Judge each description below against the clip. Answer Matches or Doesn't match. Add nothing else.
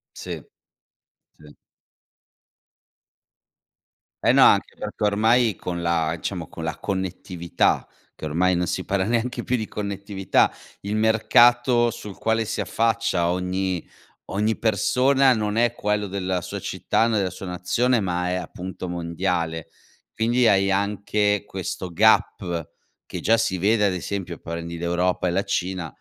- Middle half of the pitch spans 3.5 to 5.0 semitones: Matches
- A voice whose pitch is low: Matches